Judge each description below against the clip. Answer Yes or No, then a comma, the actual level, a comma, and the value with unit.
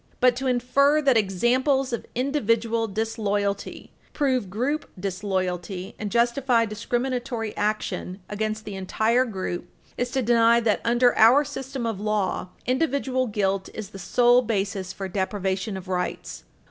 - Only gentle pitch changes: No, average, 4.1 semitones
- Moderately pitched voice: No, high, 225 Hz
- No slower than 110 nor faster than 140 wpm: Yes, slow, 135 wpm